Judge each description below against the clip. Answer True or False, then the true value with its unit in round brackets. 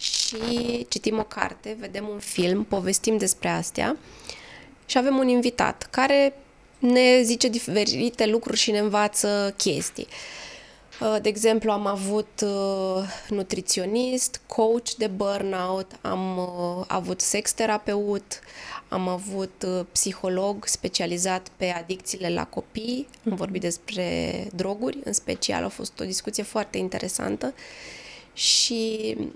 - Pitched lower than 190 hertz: False (210 Hz)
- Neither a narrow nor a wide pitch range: True (3.2 semitones)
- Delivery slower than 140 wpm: True (115 wpm)